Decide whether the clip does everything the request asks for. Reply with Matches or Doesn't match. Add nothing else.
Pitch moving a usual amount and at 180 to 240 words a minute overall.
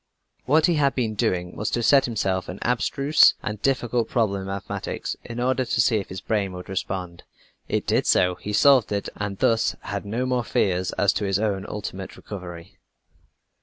Matches